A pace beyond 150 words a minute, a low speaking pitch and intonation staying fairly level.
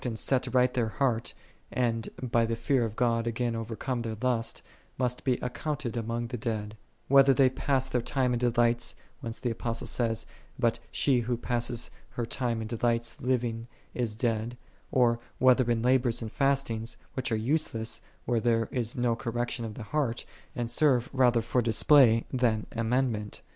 Yes: average, 180 wpm; low, 120 Hz; narrow, 1.8 semitones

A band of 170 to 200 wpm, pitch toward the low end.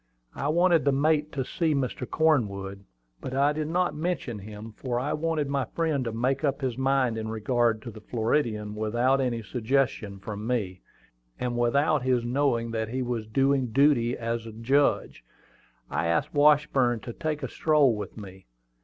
Yes: average, 175 wpm; low, 125 Hz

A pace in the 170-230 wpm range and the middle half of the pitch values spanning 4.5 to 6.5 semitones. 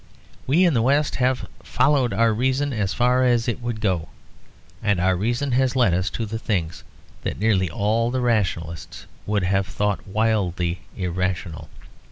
No: average, 160 wpm; average, 4.9 semitones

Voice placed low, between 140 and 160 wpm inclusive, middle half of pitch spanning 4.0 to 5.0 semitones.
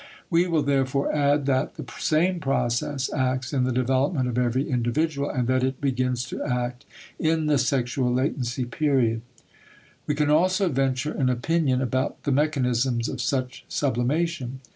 No: low, 130 Hz; average, 155 wpm; average, 2.7 semitones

